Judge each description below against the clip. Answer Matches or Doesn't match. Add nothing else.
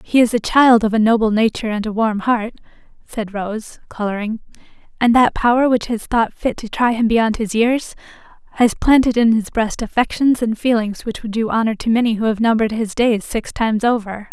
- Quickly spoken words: Matches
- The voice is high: Matches